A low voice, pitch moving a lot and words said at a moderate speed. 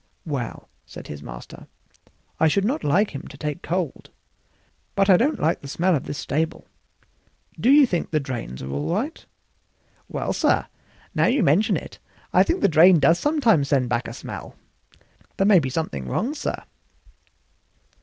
No: medium, 165 Hz; wide, 6.8 semitones; average, 170 wpm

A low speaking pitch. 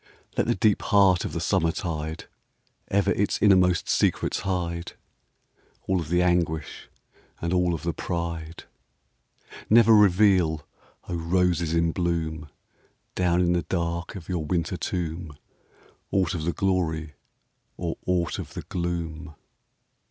Yes: very low, 85 Hz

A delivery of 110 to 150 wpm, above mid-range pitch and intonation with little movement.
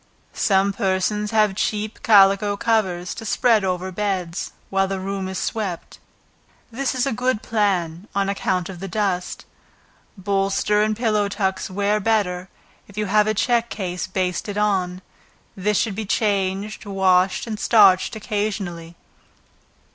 Yes: average, 140 wpm; high, 200 Hz; narrow, 2.1 semitones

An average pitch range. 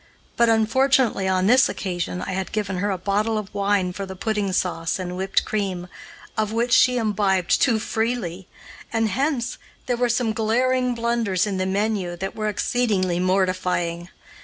Yes: average, 3.6 semitones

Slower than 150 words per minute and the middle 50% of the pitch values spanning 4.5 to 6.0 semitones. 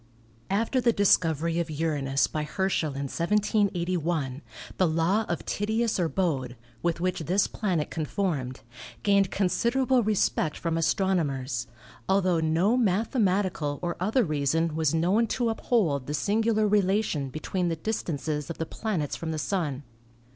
Yes: average, 140 wpm; average, 4.8 semitones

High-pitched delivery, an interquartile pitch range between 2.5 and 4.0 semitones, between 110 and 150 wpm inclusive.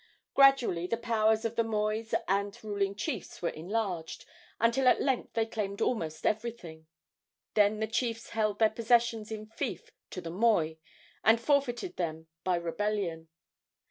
Yes: high, 215 Hz; average, 3.7 semitones; average, 145 wpm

